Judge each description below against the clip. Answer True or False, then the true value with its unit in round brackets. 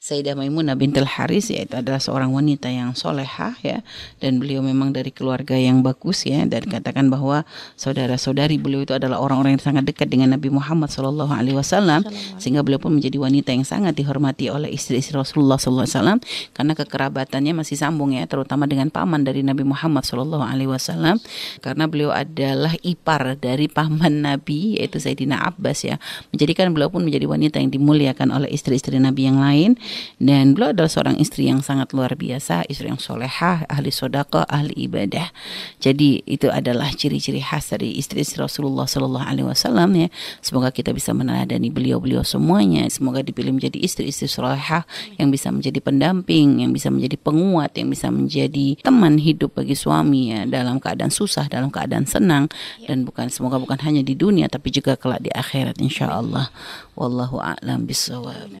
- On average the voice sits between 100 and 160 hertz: True (135 Hz)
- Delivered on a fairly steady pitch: True (2.3 semitones)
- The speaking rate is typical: False (165 wpm)